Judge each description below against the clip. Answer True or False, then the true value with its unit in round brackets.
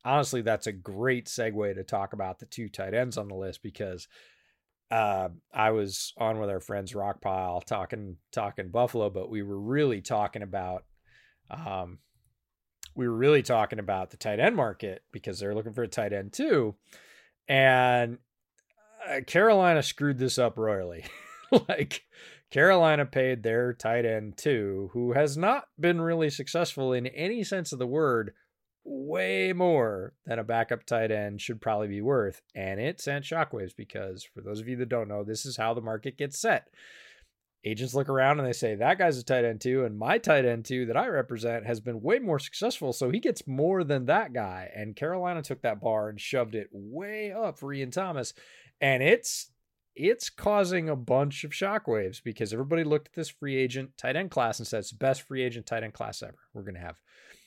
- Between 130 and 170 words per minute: False (190 wpm)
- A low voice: True (120 Hz)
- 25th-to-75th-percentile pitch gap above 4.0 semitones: True (5.1 semitones)